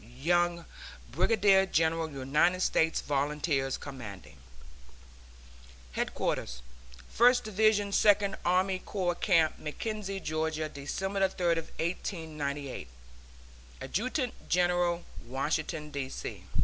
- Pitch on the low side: No, medium, 170 Hz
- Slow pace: Yes, slow, 85 wpm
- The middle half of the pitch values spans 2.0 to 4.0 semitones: No, average, 4.7 semitones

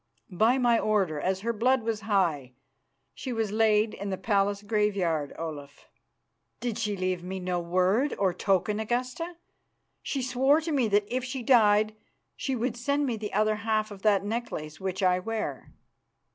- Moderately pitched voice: No, high, 210 Hz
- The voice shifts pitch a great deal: No, average, 3.9 semitones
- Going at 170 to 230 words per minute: Yes, average, 175 wpm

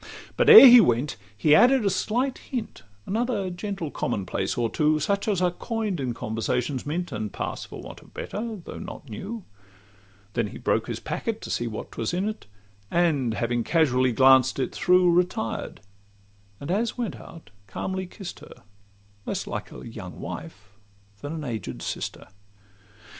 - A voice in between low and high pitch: Yes, medium, 165 Hz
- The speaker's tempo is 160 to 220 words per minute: Yes, average, 165 wpm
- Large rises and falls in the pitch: Yes, wide, 8.6 semitones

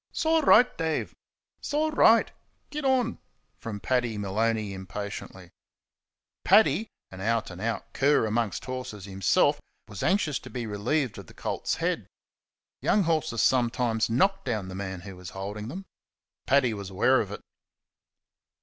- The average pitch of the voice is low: Yes, low, 115 Hz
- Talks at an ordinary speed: Yes, average, 150 wpm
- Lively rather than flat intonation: Yes, wide, 7.7 semitones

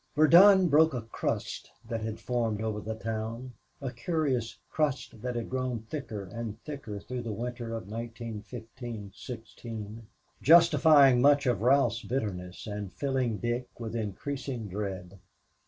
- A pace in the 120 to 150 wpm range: Yes, average, 140 wpm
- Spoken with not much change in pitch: No, average, 3.4 semitones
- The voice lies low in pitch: Yes, low, 115 Hz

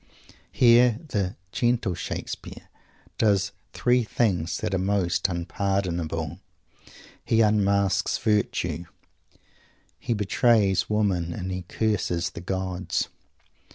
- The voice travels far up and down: No, average, 3.4 semitones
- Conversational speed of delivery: No, slow, 100 wpm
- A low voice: Yes, low, 100 Hz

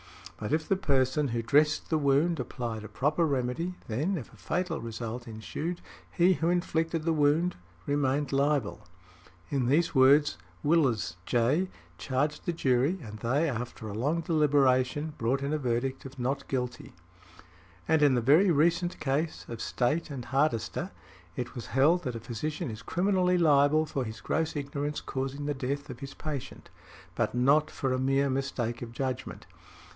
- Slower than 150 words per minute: No, average, 165 wpm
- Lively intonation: No, average, 3.9 semitones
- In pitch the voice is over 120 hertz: Yes, medium, 140 Hz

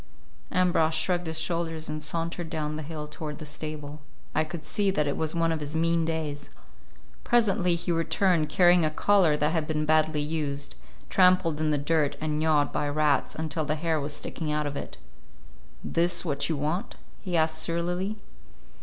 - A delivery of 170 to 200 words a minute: Yes, average, 180 wpm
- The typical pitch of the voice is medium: Yes, medium, 155 Hz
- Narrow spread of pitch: Yes, narrow, 2.0 semitones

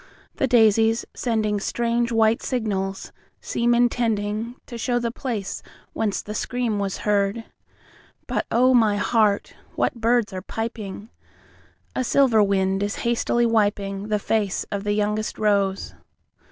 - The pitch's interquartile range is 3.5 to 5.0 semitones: No, narrow, 2.5 semitones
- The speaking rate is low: Yes, slow, 115 wpm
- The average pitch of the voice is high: Yes, high, 220 Hz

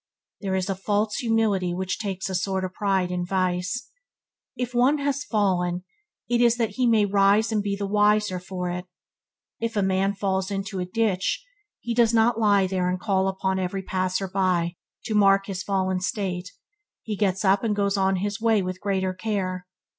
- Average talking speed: Yes, average, 190 wpm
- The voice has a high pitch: Yes, high, 195 Hz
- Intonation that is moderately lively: No, narrow, 2.2 semitones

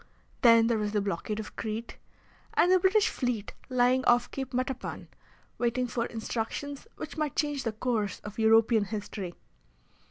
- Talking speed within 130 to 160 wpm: Yes, average, 155 wpm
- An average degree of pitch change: Yes, average, 3.0 semitones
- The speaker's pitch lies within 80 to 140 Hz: No, high, 235 Hz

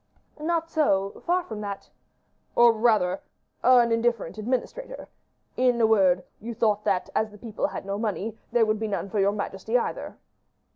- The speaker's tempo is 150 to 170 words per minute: Yes, average, 165 wpm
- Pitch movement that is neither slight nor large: Yes, average, 3.1 semitones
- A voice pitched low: No, high, 220 Hz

